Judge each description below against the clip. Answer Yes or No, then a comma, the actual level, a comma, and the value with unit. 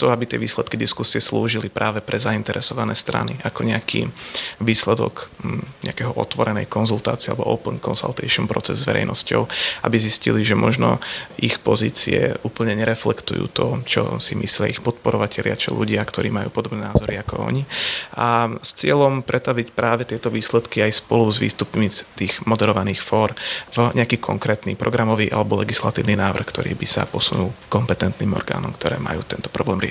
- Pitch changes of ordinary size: No, narrow, 2.0 semitones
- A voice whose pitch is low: Yes, low, 110 Hz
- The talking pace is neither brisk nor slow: Yes, average, 150 wpm